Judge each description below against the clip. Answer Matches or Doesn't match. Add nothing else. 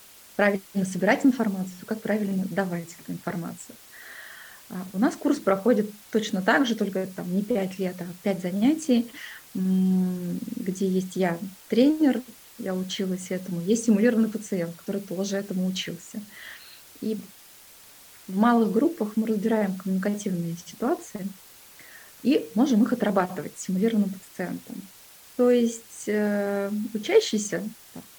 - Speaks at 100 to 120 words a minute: Matches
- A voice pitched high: Matches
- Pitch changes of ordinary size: Matches